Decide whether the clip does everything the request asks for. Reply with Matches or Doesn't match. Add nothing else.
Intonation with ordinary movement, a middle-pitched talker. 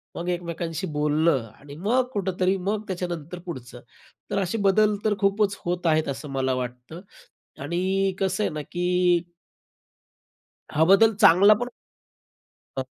Matches